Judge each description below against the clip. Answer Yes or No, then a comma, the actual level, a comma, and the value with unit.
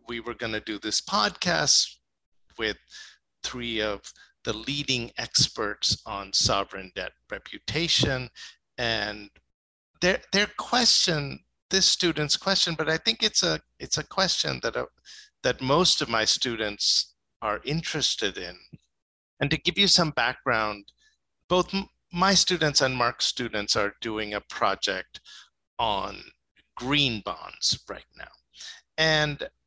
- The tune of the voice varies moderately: No, wide, 8.4 semitones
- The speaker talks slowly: Yes, slow, 130 wpm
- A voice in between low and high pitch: No, low, 130 Hz